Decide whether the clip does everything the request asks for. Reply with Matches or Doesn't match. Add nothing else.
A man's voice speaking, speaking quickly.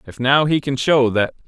Matches